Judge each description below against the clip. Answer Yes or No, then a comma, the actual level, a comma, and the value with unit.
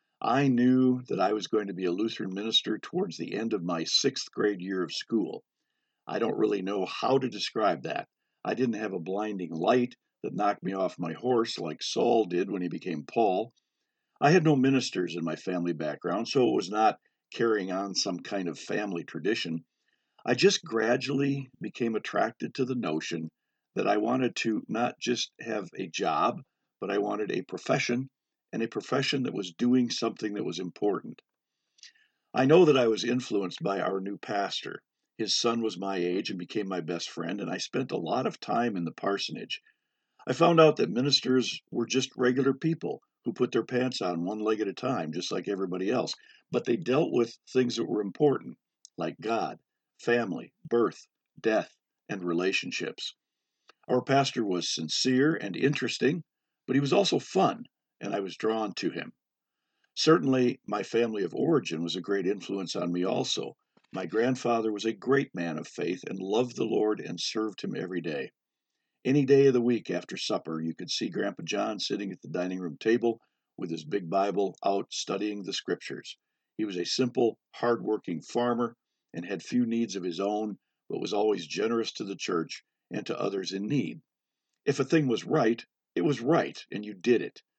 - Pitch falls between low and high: No, low, 115 Hz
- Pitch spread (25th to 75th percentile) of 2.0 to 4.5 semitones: No, average, 5.0 semitones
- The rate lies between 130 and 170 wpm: No, average, 190 wpm